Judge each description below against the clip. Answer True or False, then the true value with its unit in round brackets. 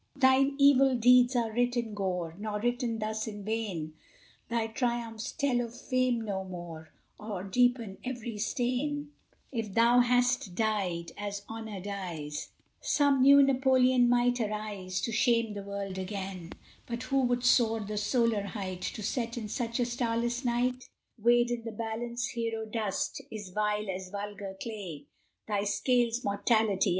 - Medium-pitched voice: False (225 Hz)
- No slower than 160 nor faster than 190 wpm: False (150 wpm)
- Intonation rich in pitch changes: False (3.3 semitones)